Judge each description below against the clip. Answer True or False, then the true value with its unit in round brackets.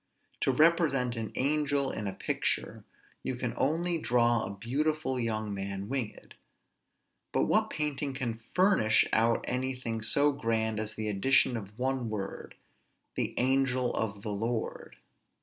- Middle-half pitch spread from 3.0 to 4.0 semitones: True (3.7 semitones)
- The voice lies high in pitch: False (125 Hz)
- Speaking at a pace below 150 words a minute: True (140 wpm)